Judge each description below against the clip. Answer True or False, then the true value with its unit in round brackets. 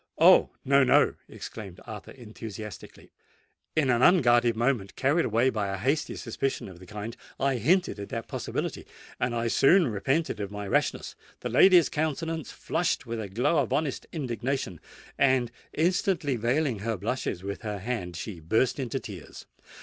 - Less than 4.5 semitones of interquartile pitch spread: False (5.0 semitones)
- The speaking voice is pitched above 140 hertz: False (120 Hz)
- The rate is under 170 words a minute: True (150 wpm)